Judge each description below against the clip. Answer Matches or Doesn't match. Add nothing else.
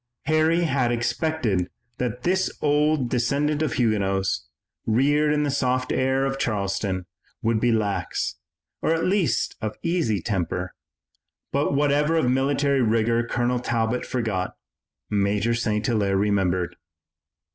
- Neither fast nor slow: Doesn't match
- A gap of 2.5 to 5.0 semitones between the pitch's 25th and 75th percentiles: Doesn't match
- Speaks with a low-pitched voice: Matches